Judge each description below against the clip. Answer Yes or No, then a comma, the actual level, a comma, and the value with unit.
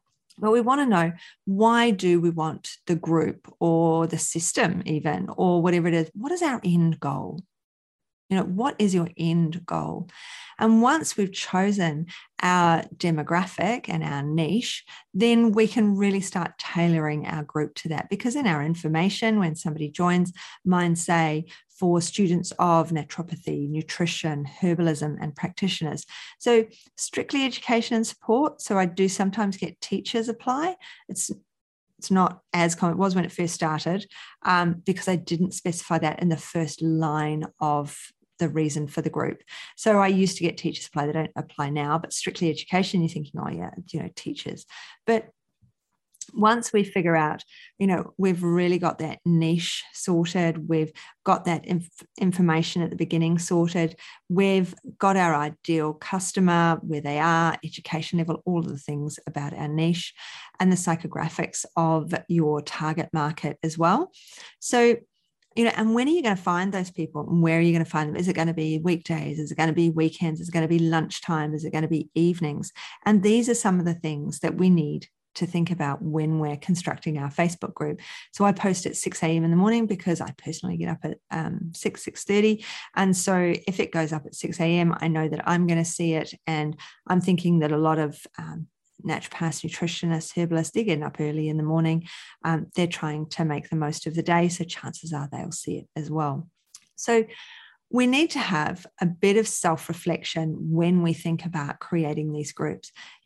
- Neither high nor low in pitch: Yes, medium, 170 Hz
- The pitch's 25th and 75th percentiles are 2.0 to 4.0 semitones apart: Yes, average, 3.0 semitones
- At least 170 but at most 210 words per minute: Yes, average, 190 wpm